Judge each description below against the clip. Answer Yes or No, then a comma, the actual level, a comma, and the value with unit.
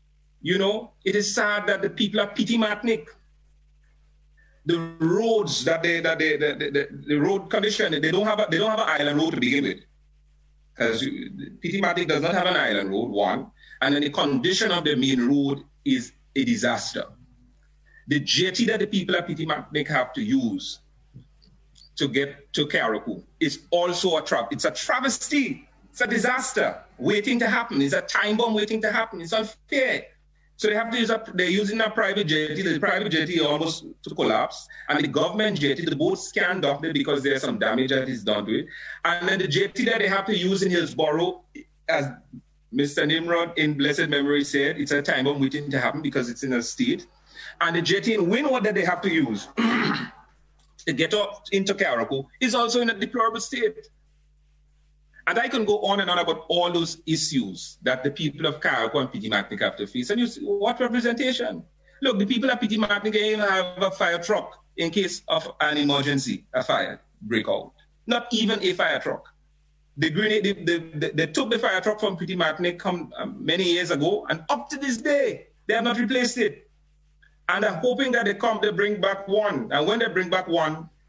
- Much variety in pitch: Yes, wide, 6.5 semitones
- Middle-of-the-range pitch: Yes, medium, 180 Hz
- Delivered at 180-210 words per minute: Yes, average, 200 wpm